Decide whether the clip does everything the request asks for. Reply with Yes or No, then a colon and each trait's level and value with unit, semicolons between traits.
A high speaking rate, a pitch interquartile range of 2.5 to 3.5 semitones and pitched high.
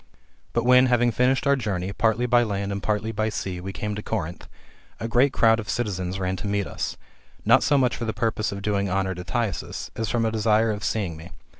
No: fast, 235 wpm; average, 3.0 semitones; low, 105 Hz